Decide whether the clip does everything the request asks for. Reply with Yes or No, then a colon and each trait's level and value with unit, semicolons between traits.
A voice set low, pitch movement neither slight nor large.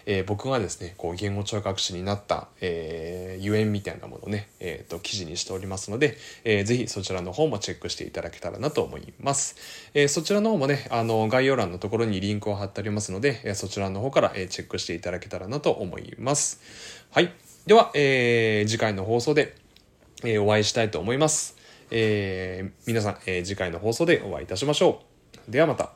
Yes: low, 105 Hz; average, 3.8 semitones